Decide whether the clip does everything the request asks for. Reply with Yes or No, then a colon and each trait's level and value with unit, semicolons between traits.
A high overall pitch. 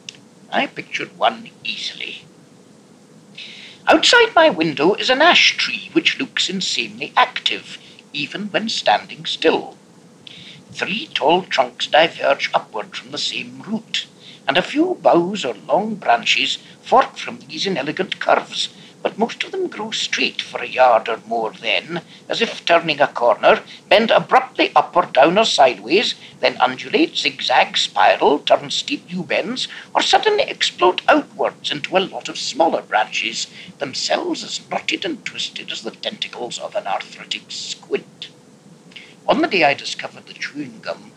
Yes: high, 225 Hz